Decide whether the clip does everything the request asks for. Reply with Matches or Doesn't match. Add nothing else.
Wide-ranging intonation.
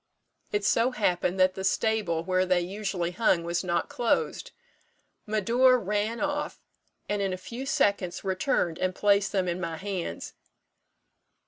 Doesn't match